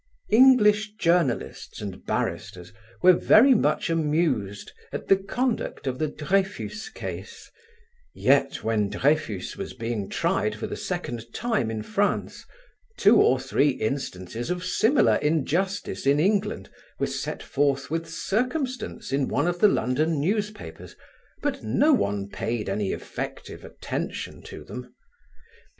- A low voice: No, medium, 155 Hz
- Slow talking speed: Yes, slow, 130 wpm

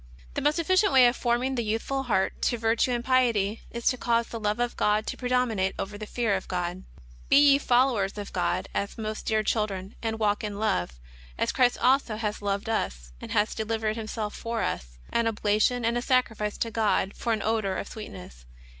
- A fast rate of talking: Yes, fast, 215 wpm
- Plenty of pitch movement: No, average, 2.8 semitones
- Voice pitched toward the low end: No, high, 220 Hz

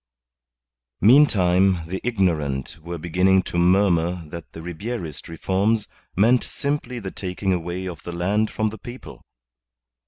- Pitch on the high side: No, very low, 95 Hz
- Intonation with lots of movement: No, average, 3.7 semitones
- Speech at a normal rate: No, slow, 130 wpm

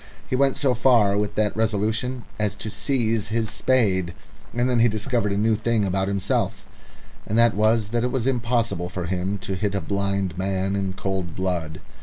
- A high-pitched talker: No, low, 105 Hz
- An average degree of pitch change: Yes, average, 3.3 semitones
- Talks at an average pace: Yes, average, 190 wpm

